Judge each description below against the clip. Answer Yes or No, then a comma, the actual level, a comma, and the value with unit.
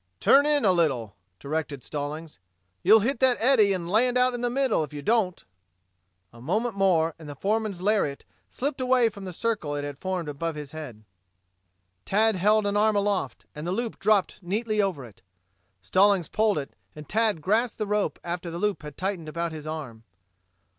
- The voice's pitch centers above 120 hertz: Yes, high, 190 Hz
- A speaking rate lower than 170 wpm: No, average, 190 wpm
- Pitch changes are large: Yes, wide, 6.0 semitones